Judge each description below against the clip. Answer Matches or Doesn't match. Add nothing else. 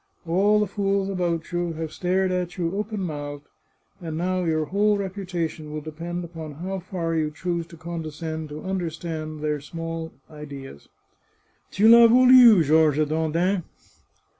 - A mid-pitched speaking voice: Matches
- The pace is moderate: Matches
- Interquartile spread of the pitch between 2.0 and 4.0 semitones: Matches